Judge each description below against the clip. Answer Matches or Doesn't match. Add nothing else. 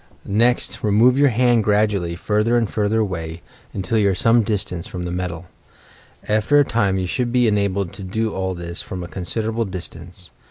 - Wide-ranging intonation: Doesn't match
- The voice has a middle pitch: Doesn't match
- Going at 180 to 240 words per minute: Matches